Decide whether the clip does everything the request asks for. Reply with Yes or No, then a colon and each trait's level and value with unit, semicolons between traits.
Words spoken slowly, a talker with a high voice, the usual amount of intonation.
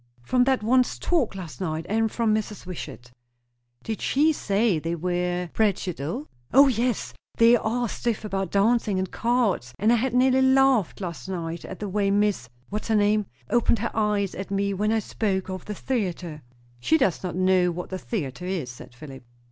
No: average, 190 wpm; high, 200 Hz; average, 4.5 semitones